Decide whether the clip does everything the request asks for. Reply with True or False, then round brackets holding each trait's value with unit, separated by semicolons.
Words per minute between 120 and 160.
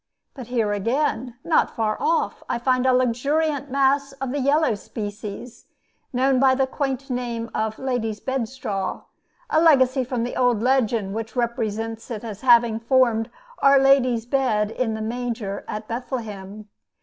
True (150 wpm)